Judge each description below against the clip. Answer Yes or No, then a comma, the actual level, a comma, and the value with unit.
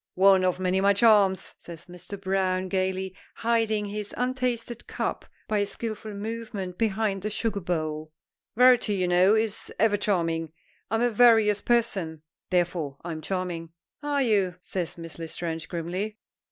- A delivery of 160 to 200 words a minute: No, average, 145 wpm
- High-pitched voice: Yes, high, 195 Hz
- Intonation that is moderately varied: Yes, average, 3.7 semitones